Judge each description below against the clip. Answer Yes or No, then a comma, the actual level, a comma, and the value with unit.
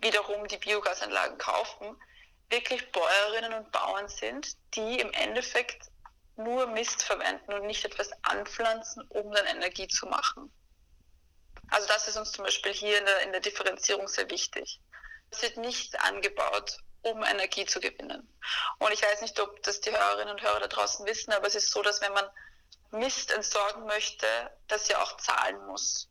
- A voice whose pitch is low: No, high, 210 Hz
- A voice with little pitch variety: Yes, narrow, 1.9 semitones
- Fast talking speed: No, average, 170 wpm